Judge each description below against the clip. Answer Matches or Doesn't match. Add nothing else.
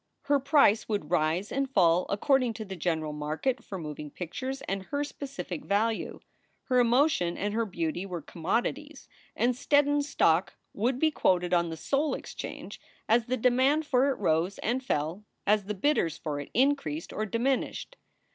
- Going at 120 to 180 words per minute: Matches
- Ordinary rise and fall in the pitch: Doesn't match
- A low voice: Doesn't match